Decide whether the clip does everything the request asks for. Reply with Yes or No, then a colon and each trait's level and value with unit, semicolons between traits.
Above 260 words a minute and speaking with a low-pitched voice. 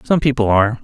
No: fast, 215 wpm; low, 120 Hz